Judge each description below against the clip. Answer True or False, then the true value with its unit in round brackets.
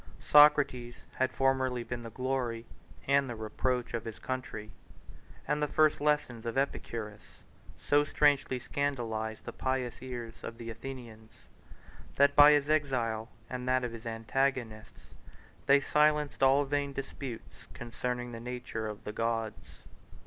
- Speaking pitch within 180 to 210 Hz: False (125 Hz)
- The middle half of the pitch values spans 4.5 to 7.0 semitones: False (3.3 semitones)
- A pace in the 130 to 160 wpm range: True (140 wpm)